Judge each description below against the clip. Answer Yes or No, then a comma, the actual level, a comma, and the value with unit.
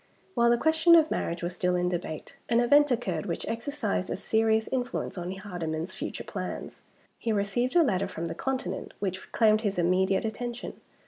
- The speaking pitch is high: Yes, high, 205 Hz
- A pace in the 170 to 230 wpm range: Yes, average, 180 wpm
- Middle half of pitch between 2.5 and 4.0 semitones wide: No, average, 5.1 semitones